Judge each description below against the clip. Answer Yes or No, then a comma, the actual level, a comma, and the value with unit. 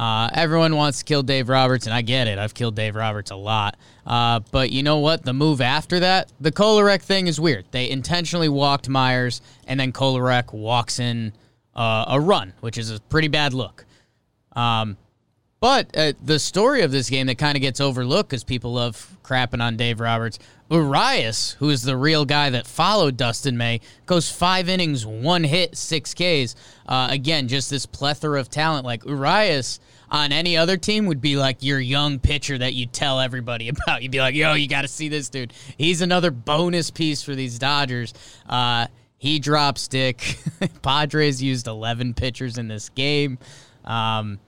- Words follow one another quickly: No, average, 190 wpm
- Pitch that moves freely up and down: No, average, 4.0 semitones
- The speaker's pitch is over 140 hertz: No, low, 135 Hz